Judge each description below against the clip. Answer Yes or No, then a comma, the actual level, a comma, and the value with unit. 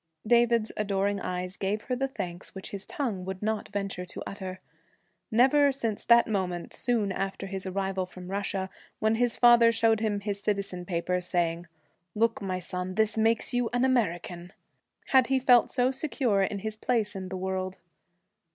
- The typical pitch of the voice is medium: No, high, 200 Hz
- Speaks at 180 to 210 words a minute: No, average, 170 wpm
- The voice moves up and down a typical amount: Yes, average, 3.7 semitones